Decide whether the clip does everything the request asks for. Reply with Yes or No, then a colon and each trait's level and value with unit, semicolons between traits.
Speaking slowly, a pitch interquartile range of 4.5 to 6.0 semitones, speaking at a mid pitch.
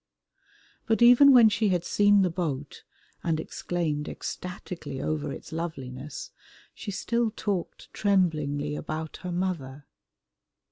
Yes: slow, 120 wpm; wide, 5.4 semitones; medium, 175 Hz